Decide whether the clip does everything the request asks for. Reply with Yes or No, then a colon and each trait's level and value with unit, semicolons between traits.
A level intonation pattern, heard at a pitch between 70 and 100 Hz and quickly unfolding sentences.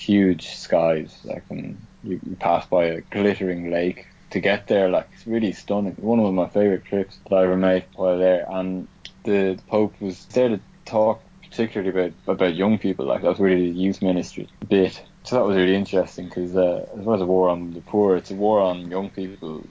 Yes: narrow, 2.1 semitones; very low, 95 Hz; fast, 215 wpm